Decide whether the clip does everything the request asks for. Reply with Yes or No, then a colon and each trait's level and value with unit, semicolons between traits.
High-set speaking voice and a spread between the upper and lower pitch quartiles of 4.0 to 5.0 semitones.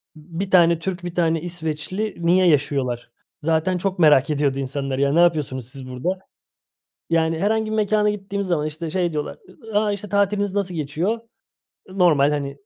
No: medium, 170 Hz; average, 4.5 semitones